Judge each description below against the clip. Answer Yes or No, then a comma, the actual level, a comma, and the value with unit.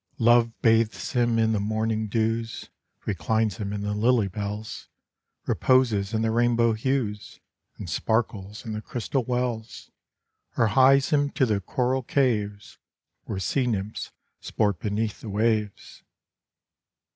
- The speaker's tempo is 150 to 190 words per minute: No, slow, 135 wpm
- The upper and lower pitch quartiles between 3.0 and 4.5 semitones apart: No, narrow, 2.4 semitones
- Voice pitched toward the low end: Yes, low, 110 Hz